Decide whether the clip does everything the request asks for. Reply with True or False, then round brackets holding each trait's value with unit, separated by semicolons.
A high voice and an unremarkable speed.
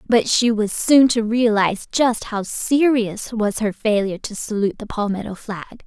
True (220 Hz; 175 wpm)